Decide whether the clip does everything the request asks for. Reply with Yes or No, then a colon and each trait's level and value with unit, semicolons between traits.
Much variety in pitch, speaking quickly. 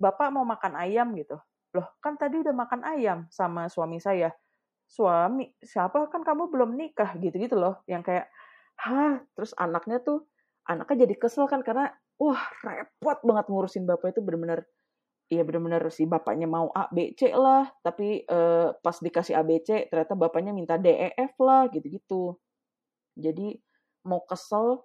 Yes: wide, 7.5 semitones; fast, 160 wpm